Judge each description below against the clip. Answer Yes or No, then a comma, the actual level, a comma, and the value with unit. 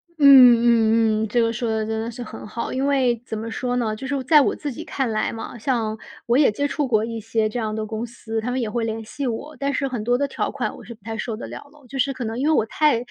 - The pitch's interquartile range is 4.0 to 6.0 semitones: No, average, 3.2 semitones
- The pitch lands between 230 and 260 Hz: Yes, high, 235 Hz